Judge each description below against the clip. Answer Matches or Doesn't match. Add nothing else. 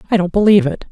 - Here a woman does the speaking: Matches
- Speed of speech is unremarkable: Doesn't match